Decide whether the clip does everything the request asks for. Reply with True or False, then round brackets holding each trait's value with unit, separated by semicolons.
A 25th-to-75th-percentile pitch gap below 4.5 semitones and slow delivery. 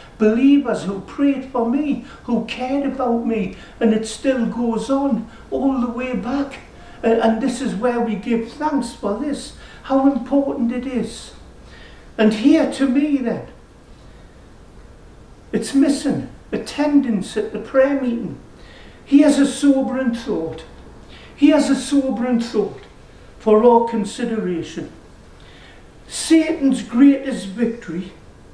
True (3.5 semitones; 125 wpm)